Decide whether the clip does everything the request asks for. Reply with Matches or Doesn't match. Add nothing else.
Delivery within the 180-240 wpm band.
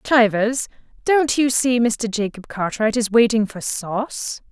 Doesn't match